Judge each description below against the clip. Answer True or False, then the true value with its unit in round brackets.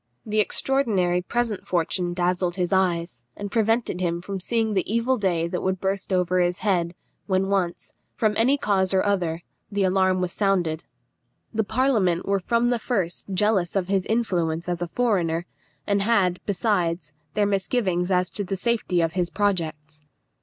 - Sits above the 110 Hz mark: True (190 Hz)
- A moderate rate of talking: True (165 wpm)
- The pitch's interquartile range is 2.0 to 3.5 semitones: True (3.0 semitones)